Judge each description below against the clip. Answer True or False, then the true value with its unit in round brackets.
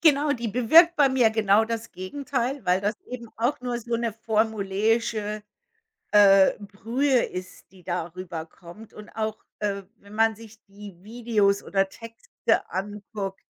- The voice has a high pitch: True (220 Hz)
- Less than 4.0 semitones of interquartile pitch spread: True (3.0 semitones)